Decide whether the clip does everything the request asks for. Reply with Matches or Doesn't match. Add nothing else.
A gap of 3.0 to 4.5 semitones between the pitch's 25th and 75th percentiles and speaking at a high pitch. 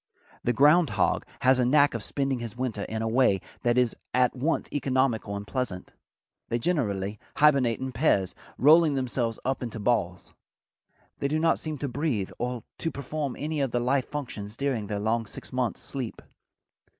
Doesn't match